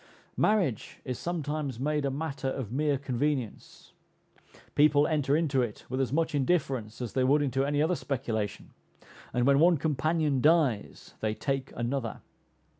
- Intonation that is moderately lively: Yes, average, 3.0 semitones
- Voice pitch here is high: No, medium, 140 Hz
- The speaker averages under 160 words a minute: Yes, average, 150 wpm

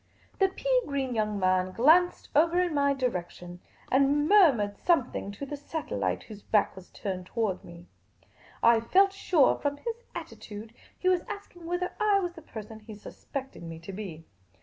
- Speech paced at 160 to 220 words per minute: Yes, average, 170 wpm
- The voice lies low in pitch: No, very high, 265 Hz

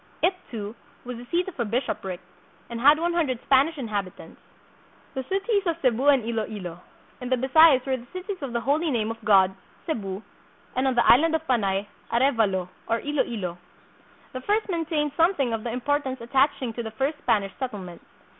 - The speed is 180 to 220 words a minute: Yes, average, 185 wpm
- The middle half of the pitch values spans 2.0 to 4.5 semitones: No, average, 5.2 semitones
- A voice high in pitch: Yes, very high, 255 Hz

